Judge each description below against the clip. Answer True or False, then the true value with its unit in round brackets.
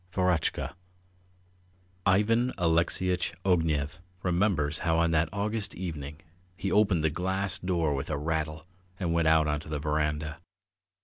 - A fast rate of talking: False (135 wpm)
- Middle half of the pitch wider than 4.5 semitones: False (3.3 semitones)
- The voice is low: True (85 Hz)